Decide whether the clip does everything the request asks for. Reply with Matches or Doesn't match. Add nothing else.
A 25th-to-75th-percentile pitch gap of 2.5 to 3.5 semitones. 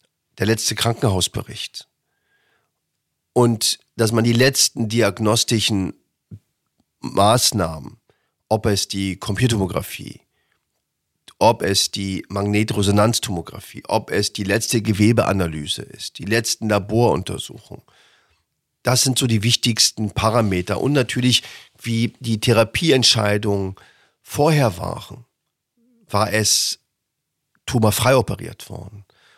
Matches